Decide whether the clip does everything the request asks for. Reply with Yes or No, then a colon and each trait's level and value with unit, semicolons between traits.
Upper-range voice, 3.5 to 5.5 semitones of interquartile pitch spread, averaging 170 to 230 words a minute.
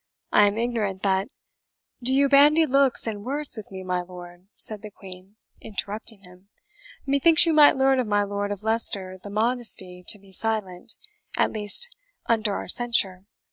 Yes: high, 210 Hz; average, 4.3 semitones; average, 175 wpm